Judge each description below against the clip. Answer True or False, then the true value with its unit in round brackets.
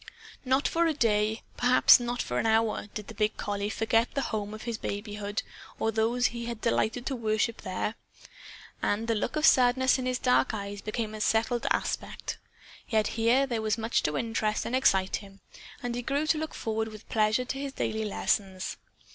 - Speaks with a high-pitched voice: True (225 Hz)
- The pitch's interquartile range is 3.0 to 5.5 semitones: False (2.5 semitones)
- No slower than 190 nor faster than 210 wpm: True (195 wpm)